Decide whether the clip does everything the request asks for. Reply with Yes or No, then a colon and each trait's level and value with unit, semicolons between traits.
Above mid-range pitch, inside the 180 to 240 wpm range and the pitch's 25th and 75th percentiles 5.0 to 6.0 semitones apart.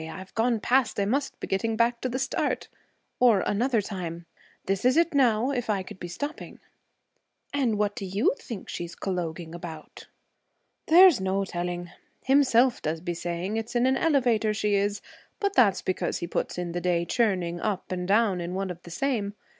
Yes: high, 205 Hz; average, 190 wpm; wide, 5.5 semitones